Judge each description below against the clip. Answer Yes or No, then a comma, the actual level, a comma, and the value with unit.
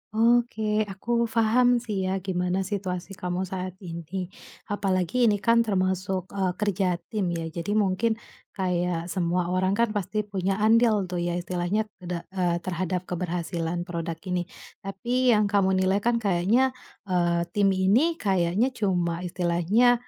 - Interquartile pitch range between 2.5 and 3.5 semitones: Yes, average, 3.1 semitones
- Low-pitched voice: No, high, 190 Hz